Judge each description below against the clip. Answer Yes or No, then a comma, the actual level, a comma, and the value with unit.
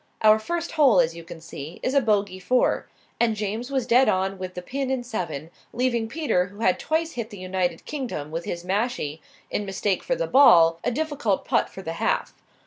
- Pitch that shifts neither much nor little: No, wide, 6.0 semitones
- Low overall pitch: No, high, 210 Hz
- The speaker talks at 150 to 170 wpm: No, fast, 205 wpm